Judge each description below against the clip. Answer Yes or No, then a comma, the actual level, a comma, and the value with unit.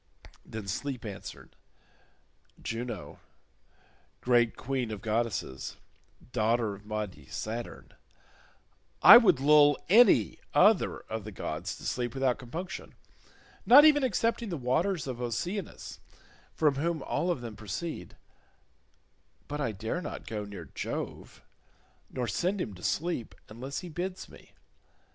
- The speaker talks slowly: Yes, slow, 125 wpm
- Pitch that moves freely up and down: Yes, wide, 7.8 semitones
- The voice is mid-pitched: No, low, 125 Hz